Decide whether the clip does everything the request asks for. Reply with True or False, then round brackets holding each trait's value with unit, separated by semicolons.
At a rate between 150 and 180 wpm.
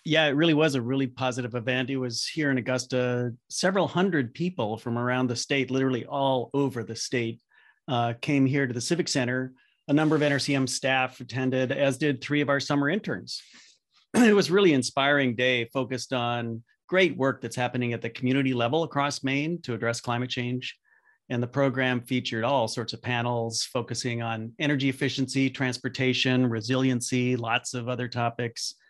True (175 wpm)